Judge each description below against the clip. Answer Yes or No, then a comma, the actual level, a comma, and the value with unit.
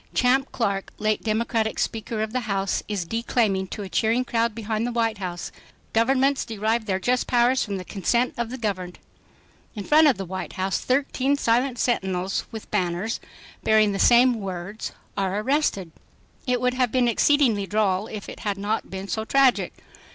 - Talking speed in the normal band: Yes, average, 175 wpm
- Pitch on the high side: Yes, high, 220 Hz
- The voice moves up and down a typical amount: Yes, average, 3.9 semitones